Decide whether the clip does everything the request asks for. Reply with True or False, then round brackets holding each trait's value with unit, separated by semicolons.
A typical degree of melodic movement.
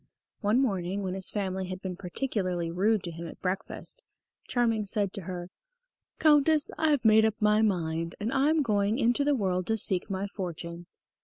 True (3.8 semitones)